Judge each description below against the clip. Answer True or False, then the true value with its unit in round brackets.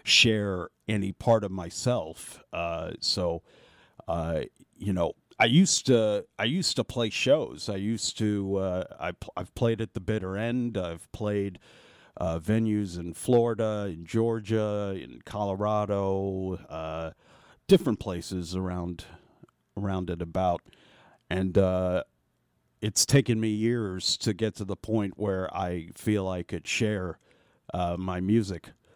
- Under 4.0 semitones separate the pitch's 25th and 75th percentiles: True (3.4 semitones)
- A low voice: True (100 Hz)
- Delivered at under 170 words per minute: True (140 wpm)